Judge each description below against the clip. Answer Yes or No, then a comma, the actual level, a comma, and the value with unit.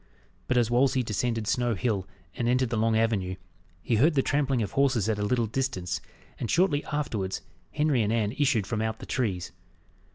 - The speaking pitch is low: Yes, low, 115 Hz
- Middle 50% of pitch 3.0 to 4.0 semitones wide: Yes, average, 3.6 semitones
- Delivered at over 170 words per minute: Yes, average, 190 wpm